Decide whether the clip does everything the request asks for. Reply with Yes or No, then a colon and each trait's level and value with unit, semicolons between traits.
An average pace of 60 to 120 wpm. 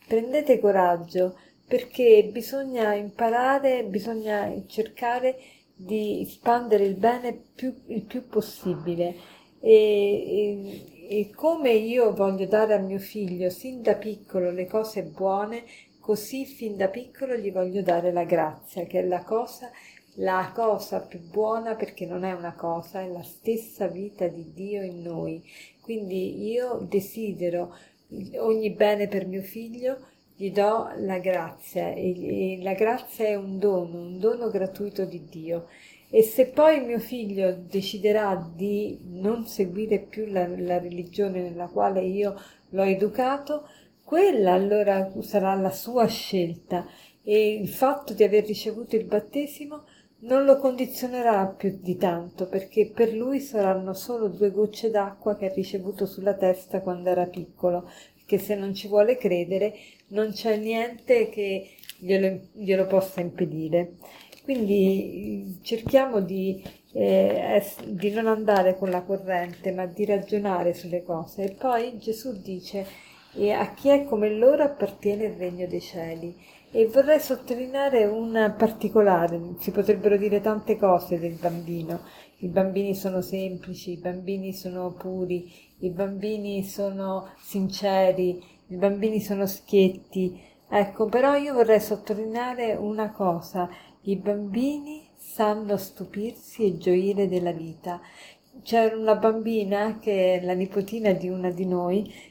No: average, 140 wpm